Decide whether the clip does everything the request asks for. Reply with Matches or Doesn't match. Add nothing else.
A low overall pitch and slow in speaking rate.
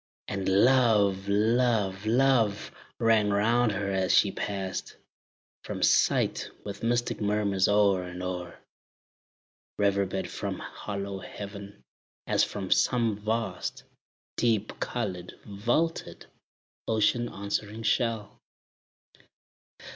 Matches